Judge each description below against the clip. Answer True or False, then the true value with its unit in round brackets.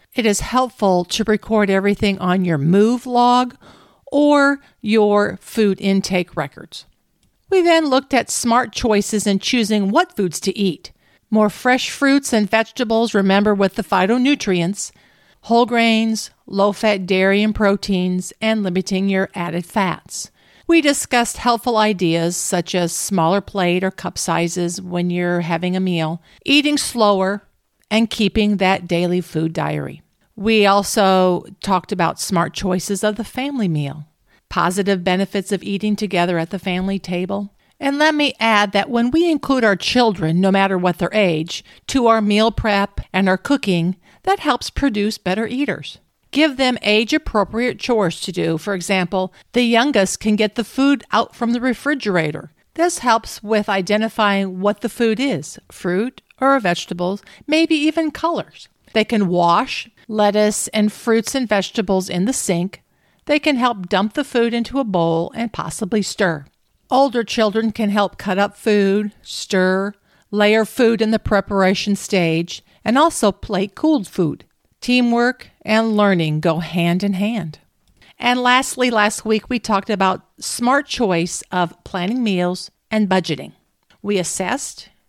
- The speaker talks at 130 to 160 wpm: True (150 wpm)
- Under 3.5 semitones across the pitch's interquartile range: False (4.0 semitones)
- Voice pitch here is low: False (205 Hz)